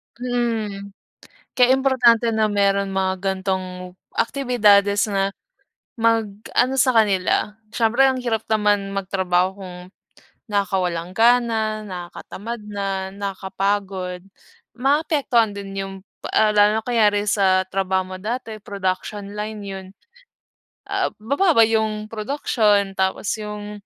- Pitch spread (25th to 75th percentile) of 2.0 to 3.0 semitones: Yes, average, 2.7 semitones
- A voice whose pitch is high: Yes, high, 205 Hz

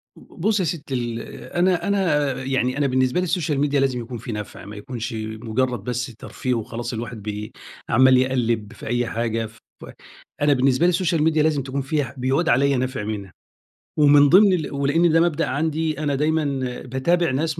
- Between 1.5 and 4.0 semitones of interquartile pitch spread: No, average, 4.7 semitones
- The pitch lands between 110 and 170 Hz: Yes, low, 135 Hz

